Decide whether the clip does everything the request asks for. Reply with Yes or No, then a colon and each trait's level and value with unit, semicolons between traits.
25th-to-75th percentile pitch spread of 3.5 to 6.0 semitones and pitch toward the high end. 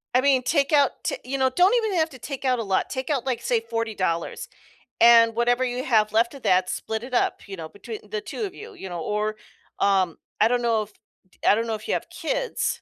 Yes: average, 3.9 semitones; high, 235 Hz